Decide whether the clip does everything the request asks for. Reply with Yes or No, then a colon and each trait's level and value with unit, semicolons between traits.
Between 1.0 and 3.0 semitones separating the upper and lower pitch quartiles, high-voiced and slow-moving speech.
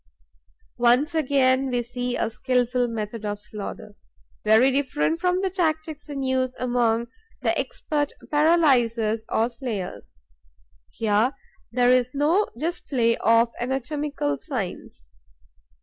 No: average, 4.1 semitones; very high, 250 Hz; slow, 115 wpm